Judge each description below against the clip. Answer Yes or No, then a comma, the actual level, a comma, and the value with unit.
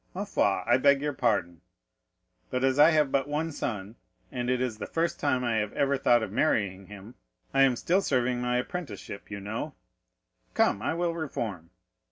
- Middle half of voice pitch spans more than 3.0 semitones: Yes, average, 5.3 semitones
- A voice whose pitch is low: Yes, low, 125 Hz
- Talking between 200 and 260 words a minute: No, average, 190 wpm